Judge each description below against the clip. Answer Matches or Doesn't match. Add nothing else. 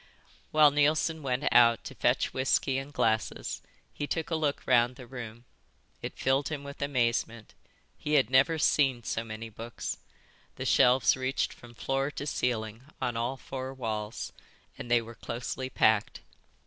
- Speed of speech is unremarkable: Matches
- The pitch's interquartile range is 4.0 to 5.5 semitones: Doesn't match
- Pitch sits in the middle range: Doesn't match